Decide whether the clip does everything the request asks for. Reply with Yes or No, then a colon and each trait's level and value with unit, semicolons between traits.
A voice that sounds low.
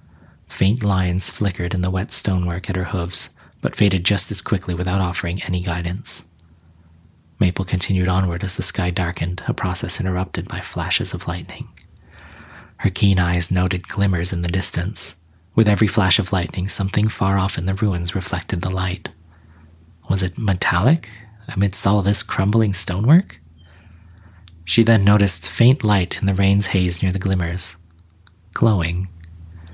Yes: very low, 95 Hz